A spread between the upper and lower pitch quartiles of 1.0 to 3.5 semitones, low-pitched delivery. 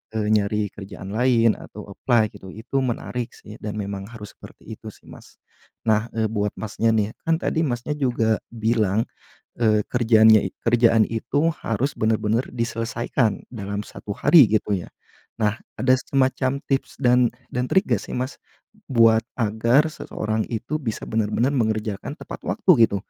Yes: narrow, 2.6 semitones; low, 115 Hz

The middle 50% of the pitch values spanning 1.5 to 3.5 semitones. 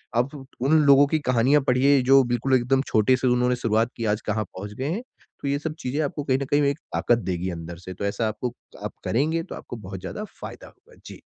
No: average, 4.3 semitones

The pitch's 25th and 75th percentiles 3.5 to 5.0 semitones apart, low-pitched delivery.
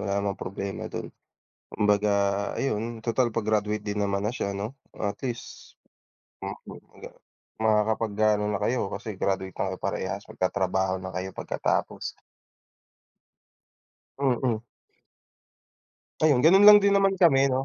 Yes: average, 3.9 semitones; low, 105 Hz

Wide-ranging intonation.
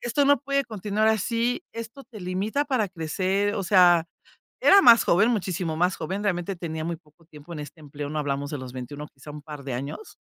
Yes: wide, 6.3 semitones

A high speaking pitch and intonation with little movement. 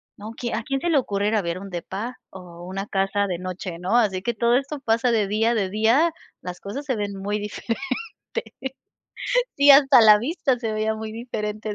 No: high, 215 Hz; average, 3.5 semitones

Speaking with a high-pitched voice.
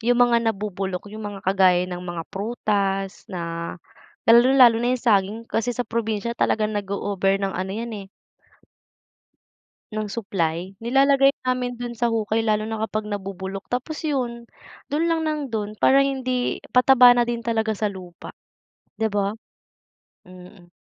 Yes: high, 215 Hz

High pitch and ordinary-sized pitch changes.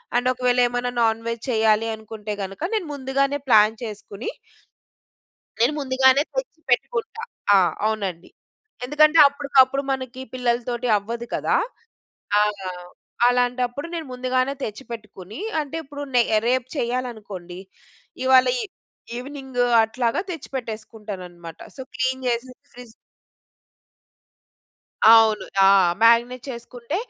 Yes: high, 245 Hz; average, 3.0 semitones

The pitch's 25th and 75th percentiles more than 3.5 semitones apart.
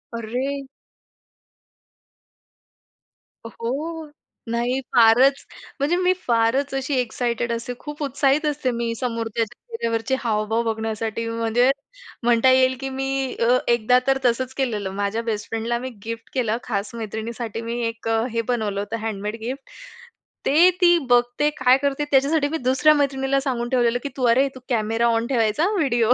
No: average, 2.9 semitones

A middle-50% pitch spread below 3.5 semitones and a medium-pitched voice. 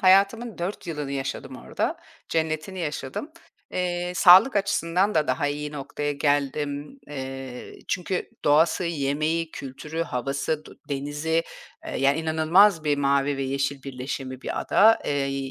No: average, 3.8 semitones; medium, 150 Hz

